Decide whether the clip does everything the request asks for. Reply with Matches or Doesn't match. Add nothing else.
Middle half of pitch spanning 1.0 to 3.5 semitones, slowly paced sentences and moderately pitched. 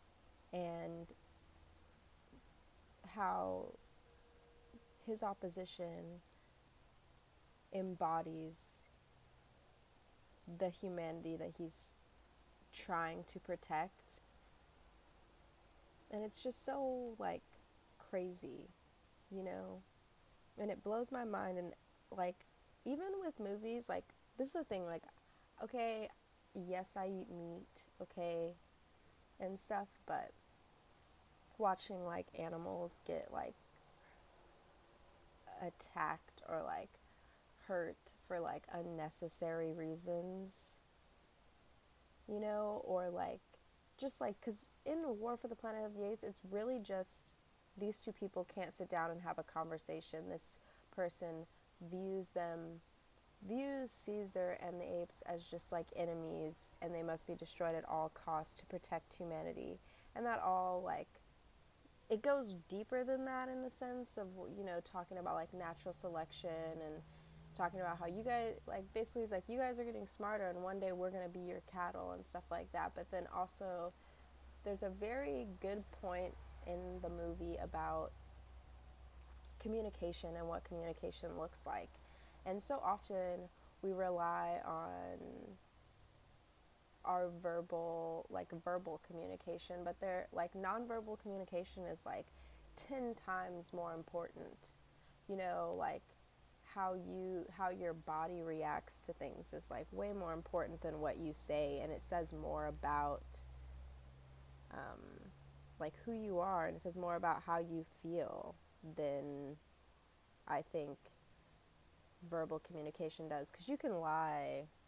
Doesn't match